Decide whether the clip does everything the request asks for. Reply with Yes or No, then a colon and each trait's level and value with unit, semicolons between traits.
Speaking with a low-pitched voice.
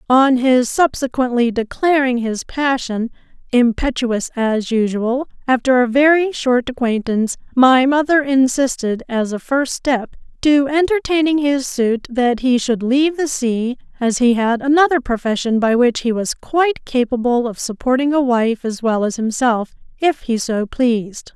No: very high, 255 Hz